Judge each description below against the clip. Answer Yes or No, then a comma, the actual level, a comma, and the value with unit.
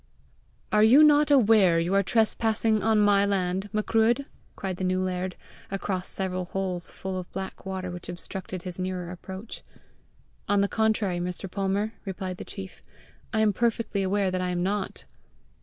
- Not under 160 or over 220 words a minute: Yes, average, 165 wpm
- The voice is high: Yes, high, 195 Hz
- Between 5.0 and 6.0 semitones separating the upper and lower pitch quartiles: No, narrow, 2.6 semitones